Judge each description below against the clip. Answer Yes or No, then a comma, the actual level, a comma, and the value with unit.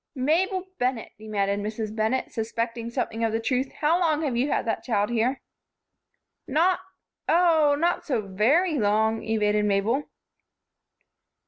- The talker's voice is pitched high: Yes, high, 235 Hz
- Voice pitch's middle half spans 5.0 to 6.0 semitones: Yes, average, 5.3 semitones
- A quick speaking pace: No, slow, 135 wpm